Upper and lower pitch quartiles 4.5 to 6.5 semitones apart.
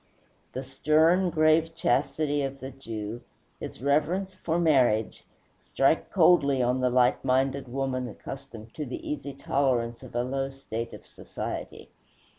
No: average, 3.4 semitones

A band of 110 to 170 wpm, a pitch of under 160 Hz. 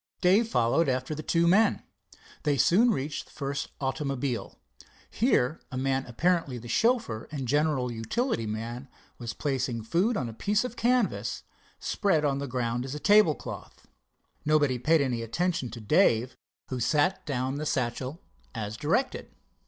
Yes: average, 155 wpm; medium, 140 Hz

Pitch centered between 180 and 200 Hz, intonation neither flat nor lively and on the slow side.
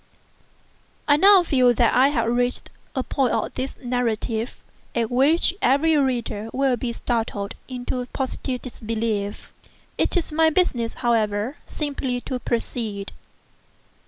No: high, 245 Hz; average, 3.0 semitones; slow, 130 wpm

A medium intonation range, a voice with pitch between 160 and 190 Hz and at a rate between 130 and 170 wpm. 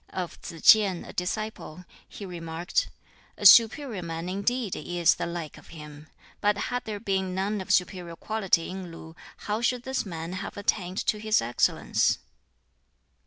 Yes: average, 3.9 semitones; medium, 185 Hz; average, 160 wpm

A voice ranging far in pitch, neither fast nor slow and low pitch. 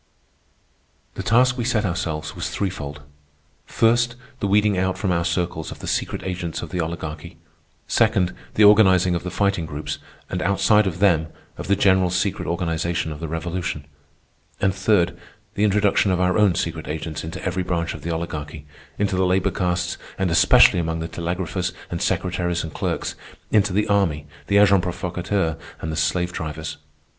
No: average, 3.1 semitones; average, 170 wpm; very low, 90 Hz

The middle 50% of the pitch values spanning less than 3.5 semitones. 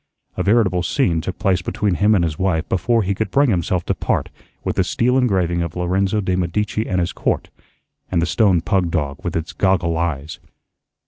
Yes: average, 3.1 semitones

